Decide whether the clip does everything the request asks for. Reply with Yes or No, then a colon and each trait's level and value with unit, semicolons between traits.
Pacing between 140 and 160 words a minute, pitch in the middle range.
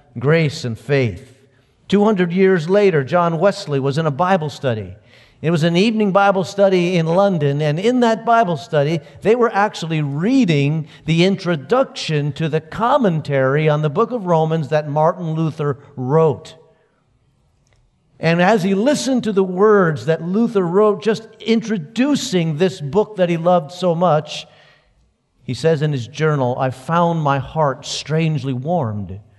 Yes: average, 150 wpm; medium, 160 Hz